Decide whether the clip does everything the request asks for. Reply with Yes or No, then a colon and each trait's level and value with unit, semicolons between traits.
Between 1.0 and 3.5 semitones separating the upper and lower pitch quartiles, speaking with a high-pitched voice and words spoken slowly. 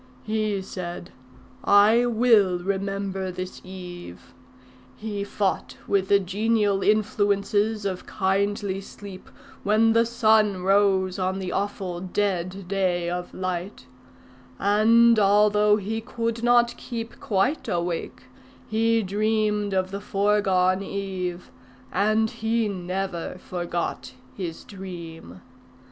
Yes: narrow, 2.5 semitones; high, 200 Hz; slow, 110 wpm